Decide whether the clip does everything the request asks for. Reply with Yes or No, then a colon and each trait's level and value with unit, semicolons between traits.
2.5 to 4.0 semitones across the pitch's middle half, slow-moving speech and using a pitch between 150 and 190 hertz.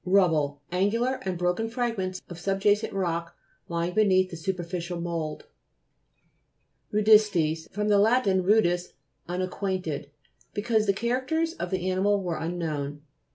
Yes: average, 3.4 semitones; slow, 130 wpm; medium, 185 Hz